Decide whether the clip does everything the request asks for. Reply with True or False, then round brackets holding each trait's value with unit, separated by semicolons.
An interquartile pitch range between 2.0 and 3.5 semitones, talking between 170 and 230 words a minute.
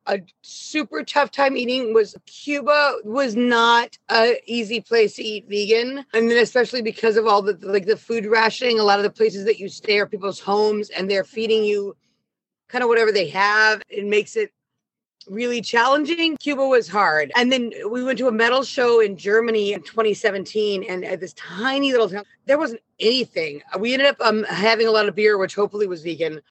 True (3.0 semitones; 200 wpm)